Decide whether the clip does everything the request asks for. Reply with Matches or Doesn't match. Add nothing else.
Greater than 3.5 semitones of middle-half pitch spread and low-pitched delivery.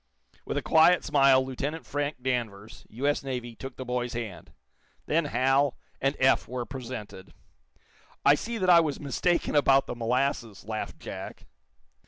Doesn't match